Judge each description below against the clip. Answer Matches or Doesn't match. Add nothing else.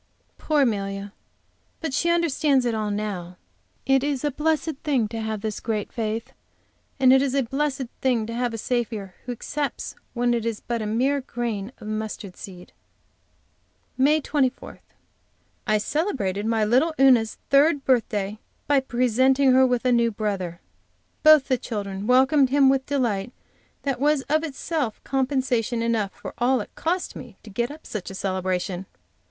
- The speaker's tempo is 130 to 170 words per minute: Matches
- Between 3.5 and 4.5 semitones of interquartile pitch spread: Matches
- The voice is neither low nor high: Doesn't match